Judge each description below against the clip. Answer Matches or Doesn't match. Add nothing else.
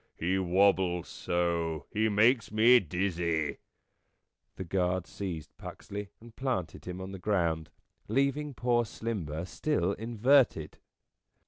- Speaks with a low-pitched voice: Matches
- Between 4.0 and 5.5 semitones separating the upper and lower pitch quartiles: Matches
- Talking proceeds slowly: Matches